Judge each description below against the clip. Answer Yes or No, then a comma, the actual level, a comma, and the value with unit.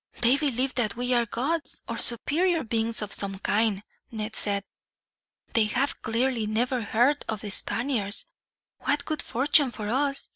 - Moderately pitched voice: No, high, 235 Hz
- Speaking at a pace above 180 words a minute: No, average, 155 wpm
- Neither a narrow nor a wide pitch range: Yes, average, 4.0 semitones